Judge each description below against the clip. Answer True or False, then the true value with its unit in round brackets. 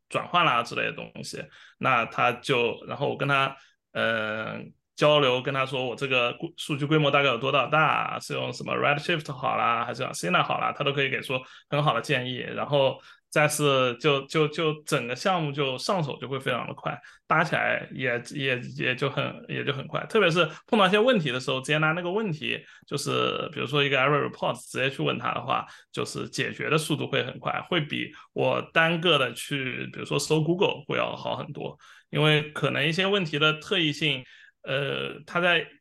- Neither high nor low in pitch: True (145 Hz)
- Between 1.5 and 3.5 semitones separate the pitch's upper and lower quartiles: True (2.5 semitones)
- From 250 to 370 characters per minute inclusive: True (325 characters per minute)